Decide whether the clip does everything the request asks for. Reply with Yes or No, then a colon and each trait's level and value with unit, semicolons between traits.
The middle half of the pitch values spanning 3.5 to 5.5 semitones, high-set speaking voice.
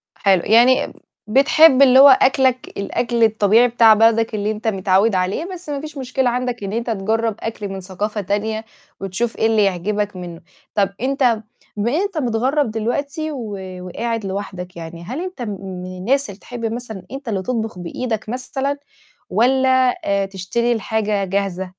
Yes: average, 4.3 semitones; high, 225 Hz